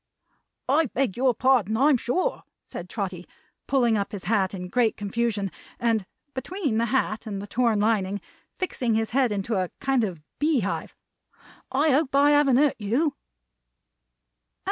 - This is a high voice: Yes, high, 235 Hz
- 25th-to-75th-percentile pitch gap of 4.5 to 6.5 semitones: Yes, average, 4.8 semitones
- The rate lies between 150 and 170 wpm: Yes, average, 155 wpm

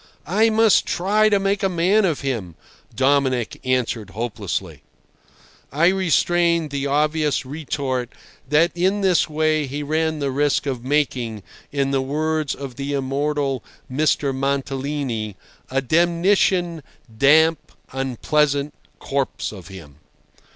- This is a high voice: No, medium, 145 Hz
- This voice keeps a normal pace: No, slow, 125 wpm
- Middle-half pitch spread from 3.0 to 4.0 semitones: Yes, average, 3.6 semitones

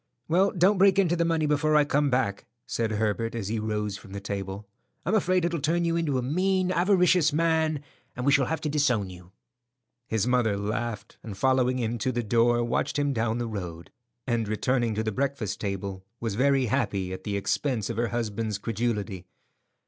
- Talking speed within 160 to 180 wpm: No, average, 195 wpm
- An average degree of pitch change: No, wide, 6.2 semitones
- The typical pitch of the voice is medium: No, low, 120 Hz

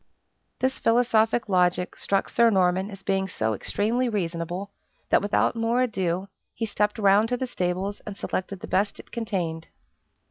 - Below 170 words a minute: Yes, average, 155 wpm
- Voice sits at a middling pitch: No, high, 200 Hz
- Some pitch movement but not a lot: Yes, average, 3.7 semitones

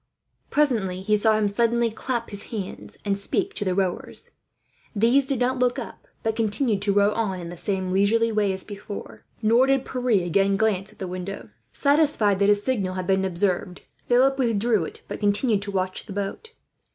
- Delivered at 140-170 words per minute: No, average, 190 wpm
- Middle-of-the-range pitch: No, high, 205 Hz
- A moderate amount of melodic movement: Yes, average, 3.5 semitones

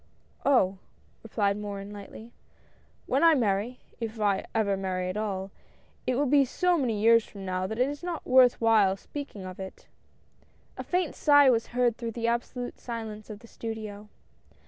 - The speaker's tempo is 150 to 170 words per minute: No, average, 185 wpm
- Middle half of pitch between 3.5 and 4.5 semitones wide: Yes, average, 3.8 semitones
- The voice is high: Yes, high, 225 Hz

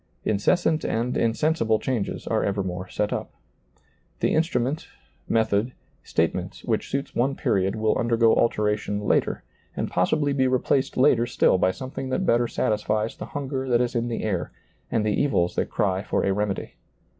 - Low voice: Yes, low, 115 Hz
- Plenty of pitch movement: No, average, 4.0 semitones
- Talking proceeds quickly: No, average, 160 wpm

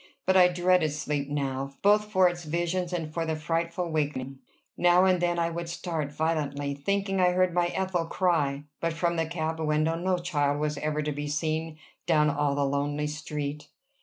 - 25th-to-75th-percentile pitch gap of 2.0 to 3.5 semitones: Yes, average, 3.0 semitones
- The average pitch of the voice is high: No, medium, 160 Hz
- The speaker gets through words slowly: No, average, 190 wpm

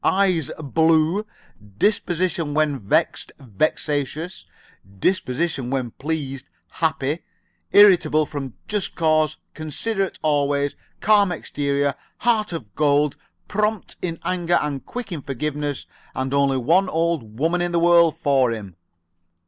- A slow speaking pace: Yes, slow, 115 wpm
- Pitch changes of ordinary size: Yes, average, 3.9 semitones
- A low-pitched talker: No, medium, 155 Hz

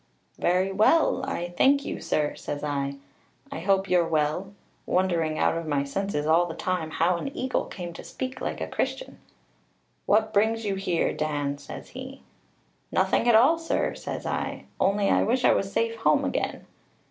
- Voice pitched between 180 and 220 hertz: Yes, high, 190 Hz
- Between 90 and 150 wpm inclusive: No, average, 175 wpm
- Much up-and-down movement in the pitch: Yes, wide, 6.0 semitones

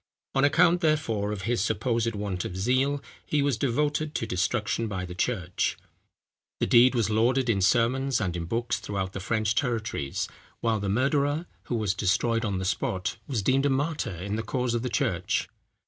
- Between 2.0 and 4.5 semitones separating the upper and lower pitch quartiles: No, average, 4.9 semitones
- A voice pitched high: No, low, 115 Hz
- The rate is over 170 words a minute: Yes, average, 185 wpm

